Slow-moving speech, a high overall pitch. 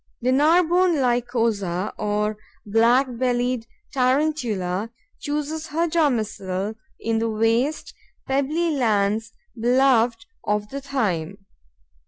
Yes: slow, 95 wpm; high, 240 Hz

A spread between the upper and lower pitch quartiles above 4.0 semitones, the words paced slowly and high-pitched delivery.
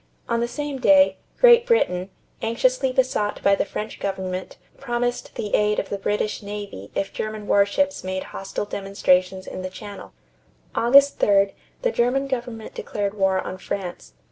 No: average, 4.6 semitones; average, 155 wpm; high, 210 Hz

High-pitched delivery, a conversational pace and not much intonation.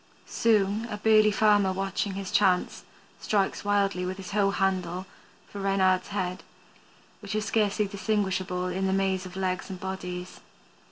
Yes: high, 195 Hz; average, 150 wpm; narrow, 1.7 semitones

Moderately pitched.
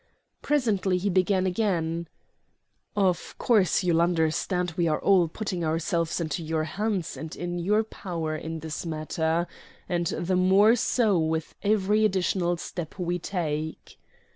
Yes: medium, 175 Hz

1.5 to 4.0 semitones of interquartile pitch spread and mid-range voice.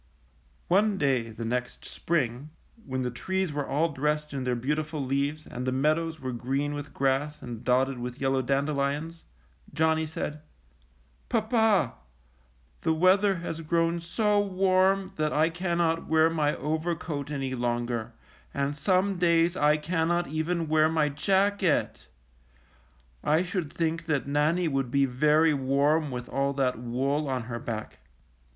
Yes: average, 3.7 semitones; medium, 150 Hz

